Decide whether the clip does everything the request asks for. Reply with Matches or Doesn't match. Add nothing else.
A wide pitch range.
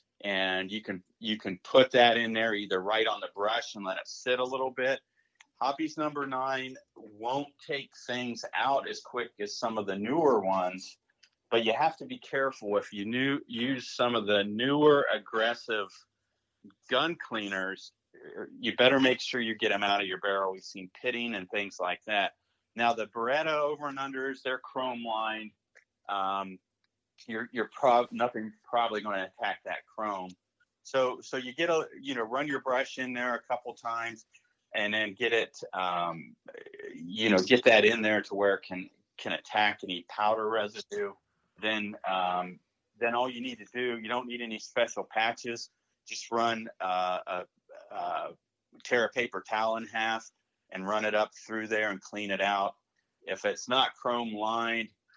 Doesn't match